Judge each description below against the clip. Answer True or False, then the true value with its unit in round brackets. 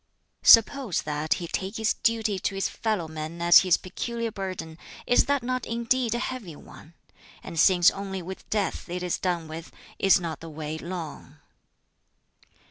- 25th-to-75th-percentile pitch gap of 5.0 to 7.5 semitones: True (5.3 semitones)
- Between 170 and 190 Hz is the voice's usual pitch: True (185 Hz)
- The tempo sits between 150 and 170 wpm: True (165 wpm)